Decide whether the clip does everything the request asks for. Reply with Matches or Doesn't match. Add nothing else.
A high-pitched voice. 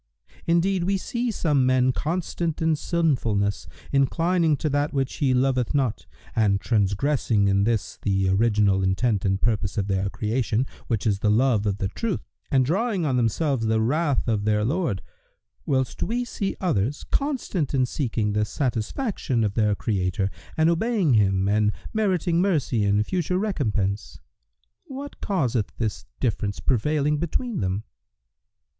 Doesn't match